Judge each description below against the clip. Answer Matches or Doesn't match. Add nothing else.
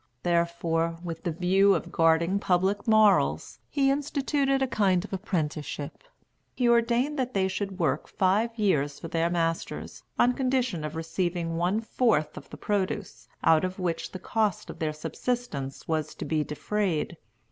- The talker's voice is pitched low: Doesn't match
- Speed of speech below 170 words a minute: Matches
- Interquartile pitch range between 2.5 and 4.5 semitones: Doesn't match